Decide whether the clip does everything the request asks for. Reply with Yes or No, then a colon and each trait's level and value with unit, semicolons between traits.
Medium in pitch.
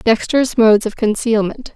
No: high, 225 Hz